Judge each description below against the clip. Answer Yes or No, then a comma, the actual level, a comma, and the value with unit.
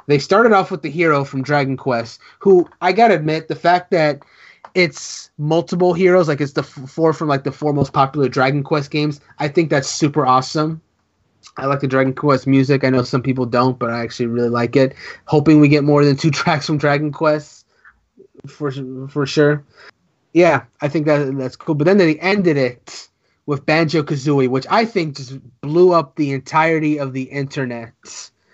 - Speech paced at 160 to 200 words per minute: Yes, average, 195 wpm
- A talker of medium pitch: Yes, medium, 145 Hz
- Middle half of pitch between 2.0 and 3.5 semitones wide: Yes, average, 3.0 semitones